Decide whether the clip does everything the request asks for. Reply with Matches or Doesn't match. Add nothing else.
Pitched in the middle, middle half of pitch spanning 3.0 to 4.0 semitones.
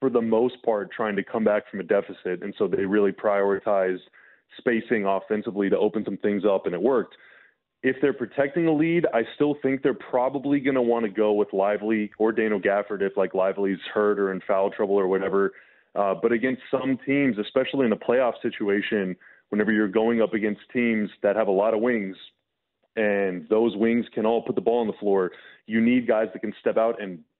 Doesn't match